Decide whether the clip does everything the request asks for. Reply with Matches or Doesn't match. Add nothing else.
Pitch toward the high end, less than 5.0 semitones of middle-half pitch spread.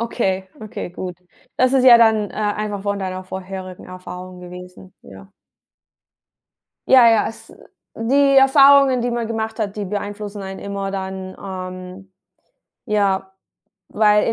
Matches